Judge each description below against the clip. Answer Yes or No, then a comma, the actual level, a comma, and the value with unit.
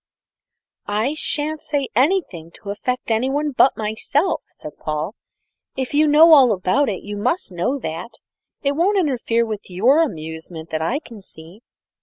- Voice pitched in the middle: No, high, 235 Hz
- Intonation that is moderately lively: No, wide, 7.7 semitones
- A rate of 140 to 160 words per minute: Yes, average, 155 wpm